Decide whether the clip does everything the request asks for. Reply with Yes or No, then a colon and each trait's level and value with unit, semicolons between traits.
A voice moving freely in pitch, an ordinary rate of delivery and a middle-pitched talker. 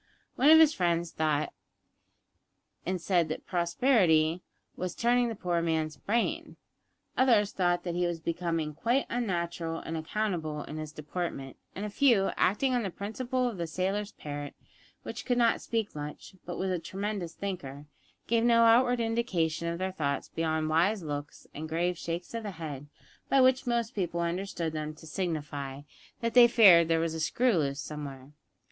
Yes: wide, 6.0 semitones; average, 170 wpm; medium, 175 Hz